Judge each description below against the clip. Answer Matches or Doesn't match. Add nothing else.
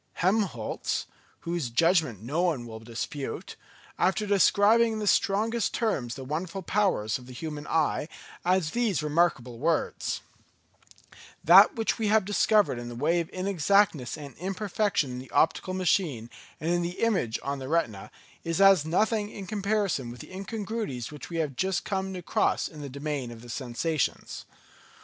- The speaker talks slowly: Doesn't match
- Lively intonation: Matches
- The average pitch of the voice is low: Doesn't match